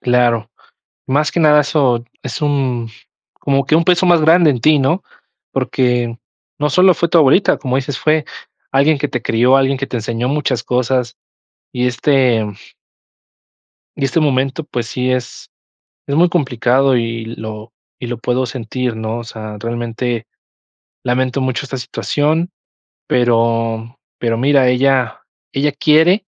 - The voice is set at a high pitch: No, low, 130 Hz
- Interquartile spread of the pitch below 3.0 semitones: No, average, 3.5 semitones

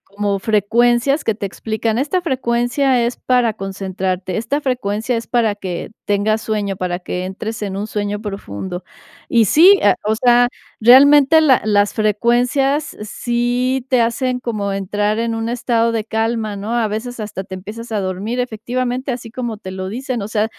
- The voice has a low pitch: No, high, 225 Hz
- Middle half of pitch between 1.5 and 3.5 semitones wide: Yes, average, 3.2 semitones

